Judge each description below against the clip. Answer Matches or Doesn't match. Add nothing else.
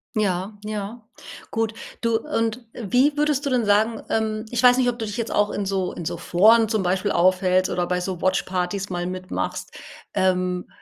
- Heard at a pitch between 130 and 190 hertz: Doesn't match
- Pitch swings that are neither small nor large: Matches